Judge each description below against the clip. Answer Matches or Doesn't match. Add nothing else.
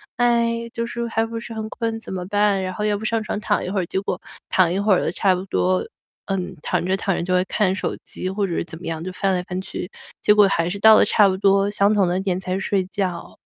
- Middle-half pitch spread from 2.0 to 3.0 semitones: Matches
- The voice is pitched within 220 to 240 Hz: Doesn't match